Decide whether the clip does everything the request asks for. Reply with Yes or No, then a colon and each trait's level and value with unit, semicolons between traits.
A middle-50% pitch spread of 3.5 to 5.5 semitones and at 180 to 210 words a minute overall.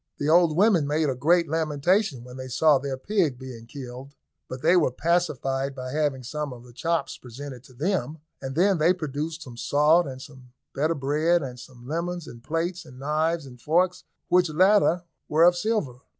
Yes: average, 4.5 semitones; average, 190 wpm